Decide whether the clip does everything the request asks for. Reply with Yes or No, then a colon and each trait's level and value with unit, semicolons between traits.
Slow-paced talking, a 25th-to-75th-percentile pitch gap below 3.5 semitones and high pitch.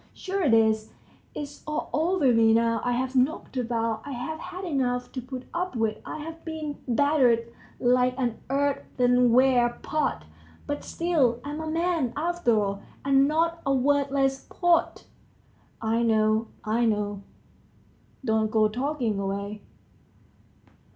No: slow, 130 wpm; average, 4.6 semitones; very high, 255 Hz